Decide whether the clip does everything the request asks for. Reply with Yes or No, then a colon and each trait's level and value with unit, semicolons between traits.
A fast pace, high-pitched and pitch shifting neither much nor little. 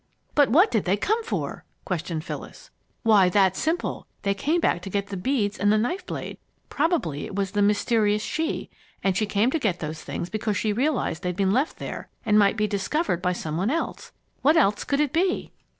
No: fast, 210 wpm; high, 210 Hz; wide, 6.9 semitones